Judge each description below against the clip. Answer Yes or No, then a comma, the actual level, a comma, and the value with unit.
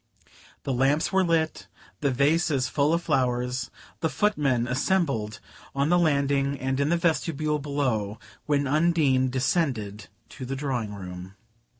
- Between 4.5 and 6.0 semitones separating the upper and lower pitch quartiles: No, average, 3.7 semitones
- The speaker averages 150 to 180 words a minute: No, average, 140 wpm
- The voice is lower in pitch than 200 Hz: Yes, medium, 140 Hz